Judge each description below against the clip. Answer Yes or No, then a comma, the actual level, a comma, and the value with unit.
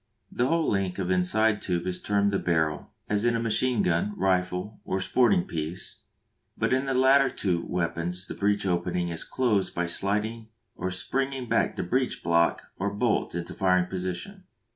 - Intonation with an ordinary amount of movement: Yes, average, 4.4 semitones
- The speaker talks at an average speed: Yes, average, 175 wpm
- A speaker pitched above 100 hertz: No, very low, 95 Hz